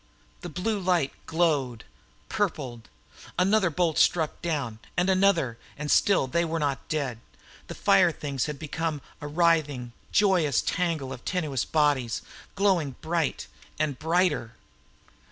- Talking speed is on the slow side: Yes, slow, 130 wpm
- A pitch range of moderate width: Yes, average, 4.4 semitones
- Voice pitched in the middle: Yes, medium, 155 Hz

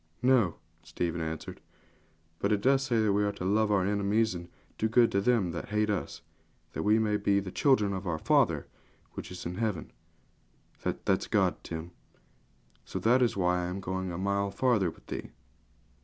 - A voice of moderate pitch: No, low, 100 Hz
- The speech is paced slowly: No, average, 185 wpm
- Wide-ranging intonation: No, average, 3.5 semitones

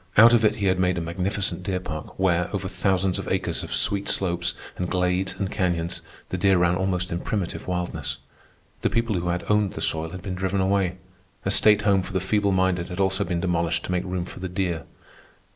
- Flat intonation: Yes, narrow, 1.7 semitones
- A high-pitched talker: No, very low, 90 Hz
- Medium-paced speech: No, fast, 220 wpm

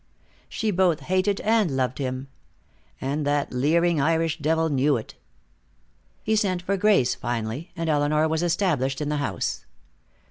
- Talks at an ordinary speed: Yes, average, 150 wpm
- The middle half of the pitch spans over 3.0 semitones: Yes, average, 4.6 semitones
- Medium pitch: Yes, medium, 155 Hz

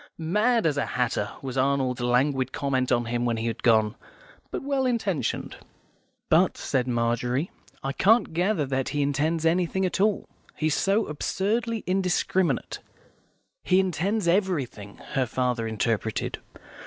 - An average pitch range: No, wide, 7.4 semitones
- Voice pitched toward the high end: No, medium, 145 Hz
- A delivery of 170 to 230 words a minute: No, average, 140 wpm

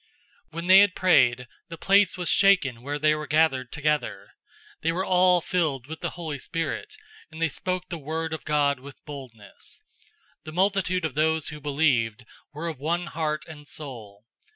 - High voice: No, medium, 155 Hz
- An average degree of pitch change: Yes, average, 3.5 semitones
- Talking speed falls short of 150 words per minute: No, average, 180 wpm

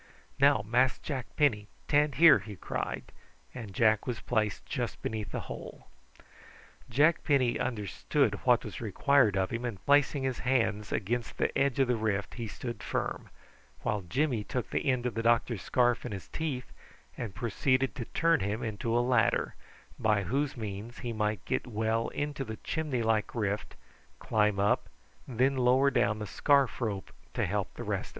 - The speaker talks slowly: No, average, 175 wpm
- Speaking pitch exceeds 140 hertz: No, low, 120 Hz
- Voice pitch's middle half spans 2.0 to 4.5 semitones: Yes, average, 3.8 semitones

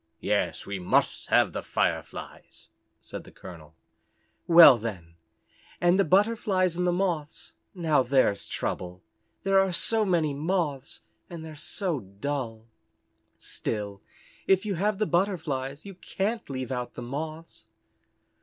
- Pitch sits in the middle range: Yes, medium, 155 Hz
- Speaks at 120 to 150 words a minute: Yes, slow, 135 wpm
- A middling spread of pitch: No, wide, 7.2 semitones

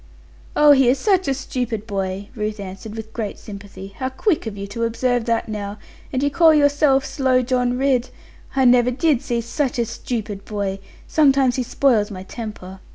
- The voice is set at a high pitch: Yes, high, 240 Hz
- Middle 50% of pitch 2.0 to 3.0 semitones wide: No, average, 4.3 semitones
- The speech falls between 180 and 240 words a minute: Yes, average, 185 wpm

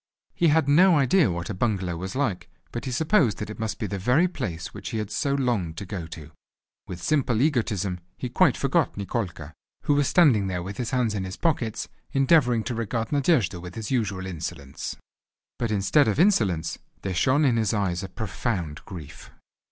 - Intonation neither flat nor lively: No, wide, 6.4 semitones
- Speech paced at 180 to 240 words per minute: Yes, average, 195 wpm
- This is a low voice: Yes, low, 110 Hz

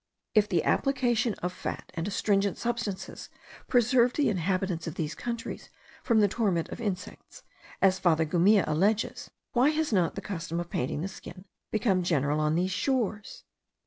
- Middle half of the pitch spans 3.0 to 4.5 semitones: No, average, 5.0 semitones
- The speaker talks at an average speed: Yes, average, 160 wpm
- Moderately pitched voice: No, high, 195 Hz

